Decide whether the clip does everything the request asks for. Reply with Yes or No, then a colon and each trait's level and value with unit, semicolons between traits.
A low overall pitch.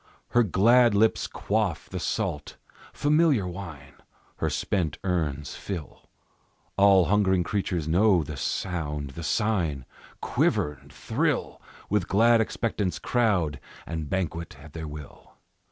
Yes: very low, 90 Hz